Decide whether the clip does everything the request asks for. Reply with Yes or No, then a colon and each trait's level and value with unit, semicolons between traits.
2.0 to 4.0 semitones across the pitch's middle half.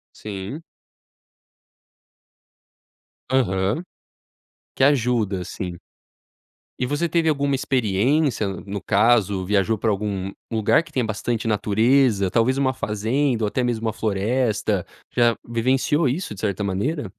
No: average, 4.6 semitones